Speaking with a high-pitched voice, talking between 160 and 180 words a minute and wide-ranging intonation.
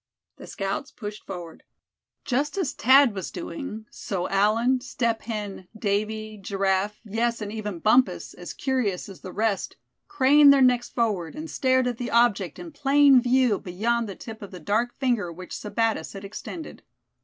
No: high, 225 Hz; average, 165 wpm; average, 4.4 semitones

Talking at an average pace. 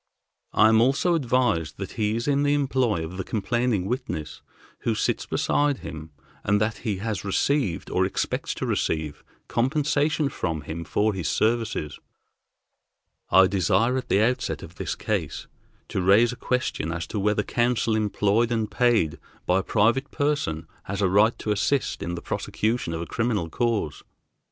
Yes: average, 165 wpm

